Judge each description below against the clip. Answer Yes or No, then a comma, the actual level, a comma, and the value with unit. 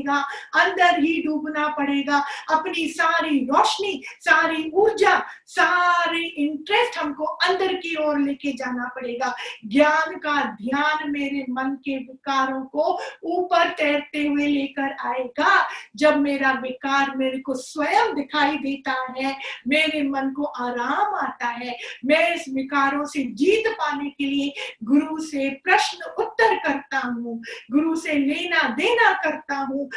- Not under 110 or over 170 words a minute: Yes, average, 130 wpm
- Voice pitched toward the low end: No, very high, 290 Hz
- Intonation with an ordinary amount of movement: Yes, average, 3.2 semitones